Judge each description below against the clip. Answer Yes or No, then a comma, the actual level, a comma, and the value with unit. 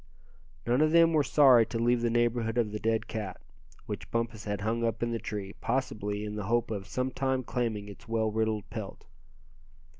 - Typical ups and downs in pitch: No, narrow, 2.2 semitones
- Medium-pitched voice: No, low, 115 Hz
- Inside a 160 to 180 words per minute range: No, average, 190 wpm